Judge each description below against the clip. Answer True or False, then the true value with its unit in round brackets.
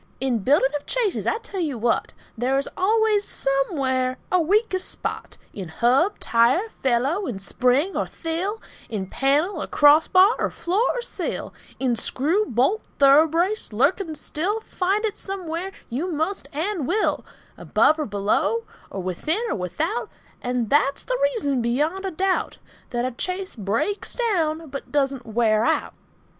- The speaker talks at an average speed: True (155 wpm)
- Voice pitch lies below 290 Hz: False (305 Hz)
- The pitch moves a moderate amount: False (7.2 semitones)